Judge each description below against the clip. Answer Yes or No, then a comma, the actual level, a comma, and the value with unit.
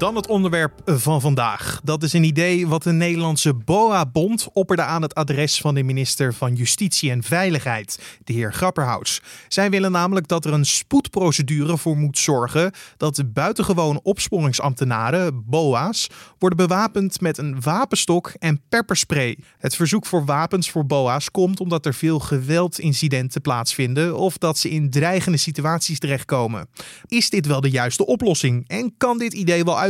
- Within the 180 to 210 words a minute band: No, average, 160 wpm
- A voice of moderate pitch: Yes, medium, 160 Hz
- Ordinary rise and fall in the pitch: Yes, average, 4.4 semitones